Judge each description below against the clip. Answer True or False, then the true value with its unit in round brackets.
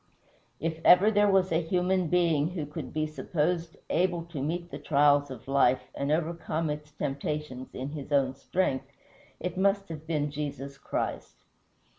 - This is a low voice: False (155 Hz)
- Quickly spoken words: False (160 wpm)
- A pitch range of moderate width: True (3.5 semitones)